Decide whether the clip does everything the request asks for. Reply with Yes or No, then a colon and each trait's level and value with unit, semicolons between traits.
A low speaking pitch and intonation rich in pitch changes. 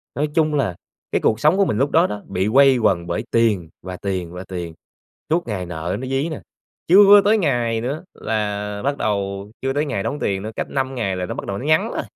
Yes: low, 115 Hz; wide, 6.6 semitones